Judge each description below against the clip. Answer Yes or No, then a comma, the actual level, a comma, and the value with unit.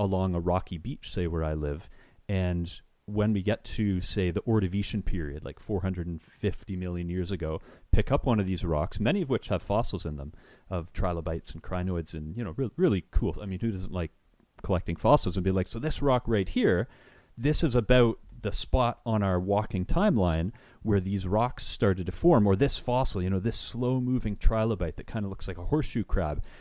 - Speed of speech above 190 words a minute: Yes, fast, 205 wpm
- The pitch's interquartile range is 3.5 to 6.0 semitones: Yes, average, 4.1 semitones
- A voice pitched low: Yes, very low, 95 Hz